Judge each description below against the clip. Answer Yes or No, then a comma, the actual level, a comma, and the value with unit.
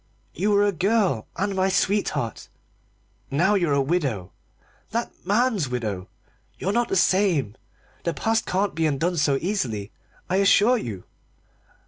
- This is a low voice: No, medium, 180 Hz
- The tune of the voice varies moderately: No, wide, 6.8 semitones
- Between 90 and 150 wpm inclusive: Yes, average, 140 wpm